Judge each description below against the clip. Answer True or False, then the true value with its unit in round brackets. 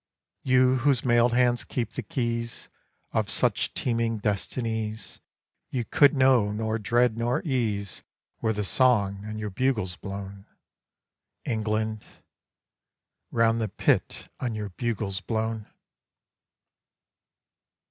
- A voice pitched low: True (115 Hz)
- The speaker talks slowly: True (110 wpm)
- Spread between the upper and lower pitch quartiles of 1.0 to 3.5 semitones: True (2.5 semitones)